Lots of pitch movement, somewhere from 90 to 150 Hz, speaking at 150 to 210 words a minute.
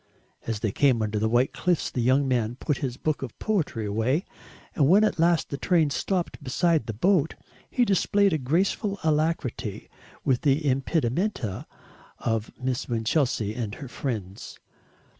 Yes: wide, 6.2 semitones; low, 135 Hz; average, 160 wpm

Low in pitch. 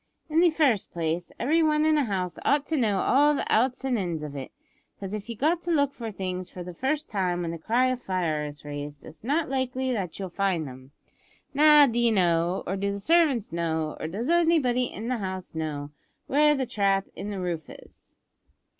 No: high, 205 Hz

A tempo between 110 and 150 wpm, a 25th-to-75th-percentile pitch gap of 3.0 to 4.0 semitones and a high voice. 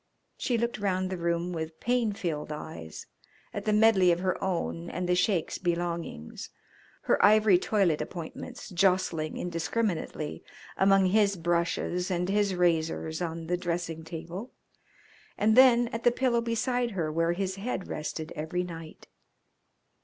No: average, 145 wpm; average, 3.6 semitones; medium, 180 Hz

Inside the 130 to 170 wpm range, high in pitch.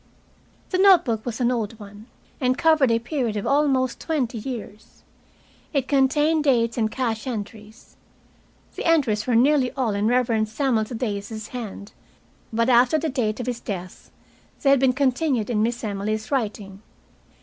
Yes: average, 160 wpm; high, 240 Hz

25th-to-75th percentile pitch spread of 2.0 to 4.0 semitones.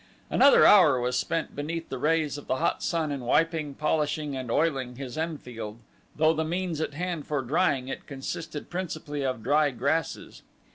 Yes: average, 3.5 semitones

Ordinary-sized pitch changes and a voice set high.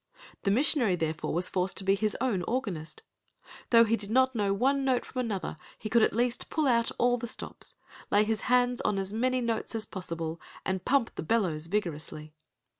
Yes: average, 4.6 semitones; high, 220 Hz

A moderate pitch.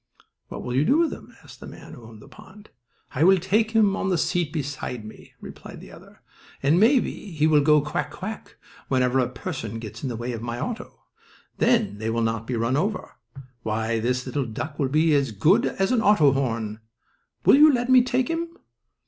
Yes: medium, 145 Hz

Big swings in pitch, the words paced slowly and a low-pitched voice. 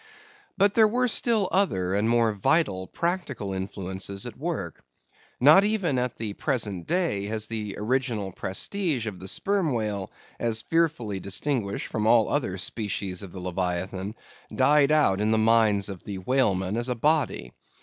No: wide, 7.1 semitones; average, 160 wpm; low, 110 Hz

